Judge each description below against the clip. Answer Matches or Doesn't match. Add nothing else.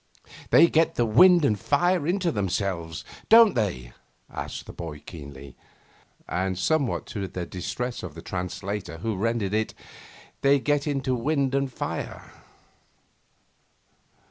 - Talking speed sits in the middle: Doesn't match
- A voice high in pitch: Doesn't match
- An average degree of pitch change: Doesn't match